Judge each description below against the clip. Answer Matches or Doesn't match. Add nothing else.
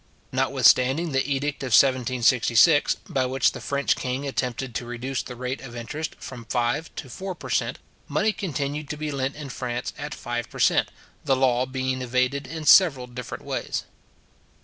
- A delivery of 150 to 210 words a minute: Matches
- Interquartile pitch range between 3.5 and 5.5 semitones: Doesn't match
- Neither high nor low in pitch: Doesn't match